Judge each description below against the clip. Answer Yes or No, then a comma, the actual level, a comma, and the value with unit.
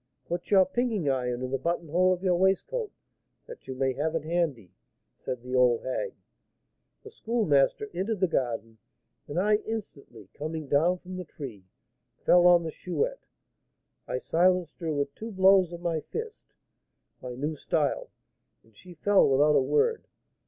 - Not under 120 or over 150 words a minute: No, average, 160 wpm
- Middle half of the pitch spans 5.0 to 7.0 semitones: Yes, wide, 5.6 semitones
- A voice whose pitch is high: No, medium, 170 Hz